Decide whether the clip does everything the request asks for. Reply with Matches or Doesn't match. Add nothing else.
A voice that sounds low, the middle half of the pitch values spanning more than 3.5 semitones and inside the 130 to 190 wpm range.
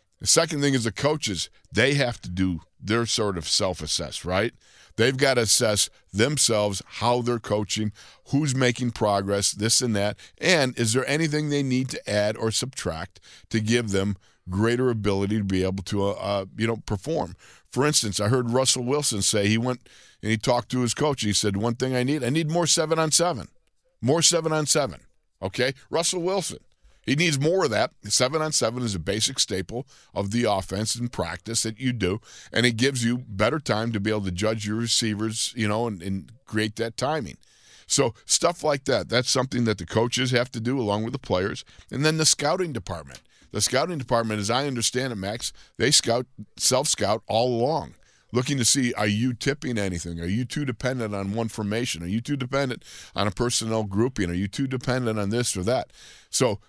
Doesn't match